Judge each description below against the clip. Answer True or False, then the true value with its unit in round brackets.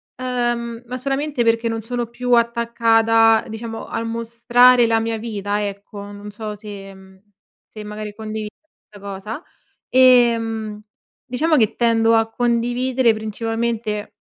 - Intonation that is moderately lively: False (1.9 semitones)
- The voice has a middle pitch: False (225 Hz)